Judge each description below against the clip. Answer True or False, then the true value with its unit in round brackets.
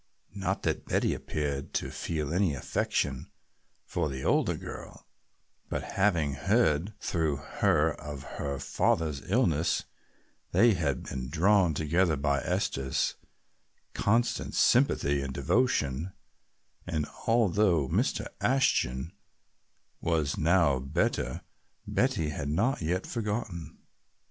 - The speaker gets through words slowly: True (110 wpm)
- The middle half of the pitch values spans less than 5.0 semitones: False (5.3 semitones)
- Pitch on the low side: True (80 Hz)